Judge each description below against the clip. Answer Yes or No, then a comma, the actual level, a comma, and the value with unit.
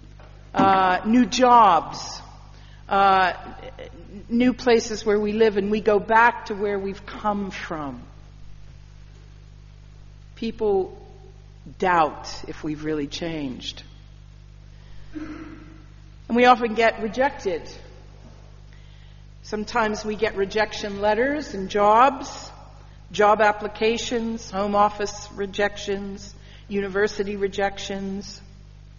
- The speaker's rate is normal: No, slow, 90 wpm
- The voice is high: Yes, high, 200 Hz